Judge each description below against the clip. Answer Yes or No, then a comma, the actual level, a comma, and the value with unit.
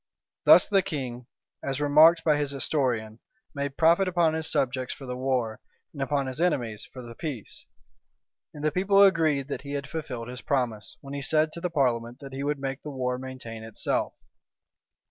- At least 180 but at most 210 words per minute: Yes, average, 185 wpm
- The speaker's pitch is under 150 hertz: Yes, medium, 140 Hz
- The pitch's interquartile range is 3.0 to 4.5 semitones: Yes, average, 3.6 semitones